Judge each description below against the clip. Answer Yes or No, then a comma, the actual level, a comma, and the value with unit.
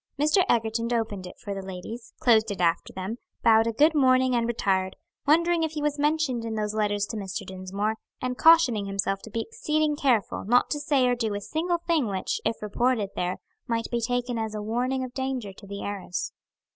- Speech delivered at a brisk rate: Yes, fast, 210 wpm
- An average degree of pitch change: Yes, average, 4.5 semitones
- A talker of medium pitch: No, high, 230 Hz